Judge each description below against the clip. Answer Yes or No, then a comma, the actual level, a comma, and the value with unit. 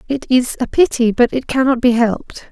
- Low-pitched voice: No, very high, 250 Hz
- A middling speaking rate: No, fast, 215 wpm